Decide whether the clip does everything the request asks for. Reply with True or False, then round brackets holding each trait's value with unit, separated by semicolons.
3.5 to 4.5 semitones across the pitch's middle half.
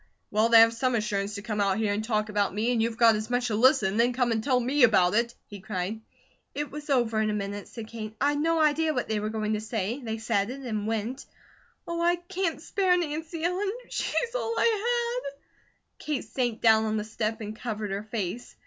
False (5.3 semitones)